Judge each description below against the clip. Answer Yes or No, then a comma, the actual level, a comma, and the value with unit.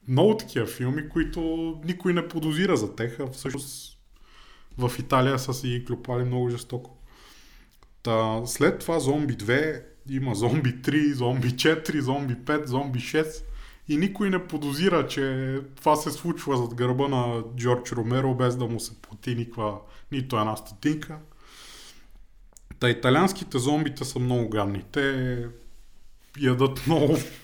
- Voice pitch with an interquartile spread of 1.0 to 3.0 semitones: No, average, 3.7 semitones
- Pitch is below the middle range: Yes, low, 130 Hz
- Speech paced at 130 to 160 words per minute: Yes, average, 135 wpm